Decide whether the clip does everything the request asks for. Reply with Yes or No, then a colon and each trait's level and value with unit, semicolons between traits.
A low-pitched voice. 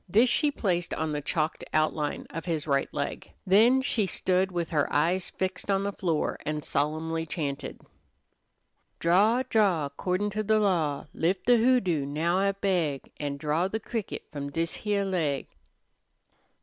No: medium, 175 Hz